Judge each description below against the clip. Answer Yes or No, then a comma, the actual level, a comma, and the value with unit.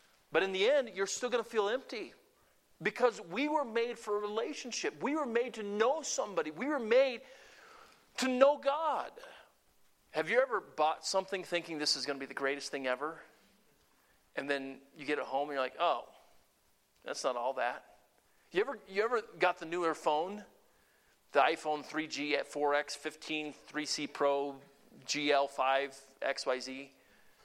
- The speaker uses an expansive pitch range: Yes, wide, 8.9 semitones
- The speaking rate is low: No, average, 165 wpm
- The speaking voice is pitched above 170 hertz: No, medium, 165 Hz